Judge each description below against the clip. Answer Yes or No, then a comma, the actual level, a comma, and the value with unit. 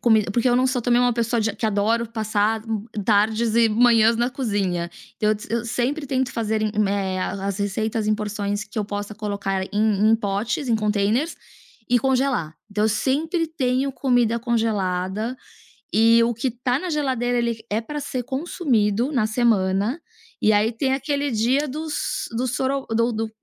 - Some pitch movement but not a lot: Yes, average, 3.0 semitones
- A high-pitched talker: Yes, high, 225 Hz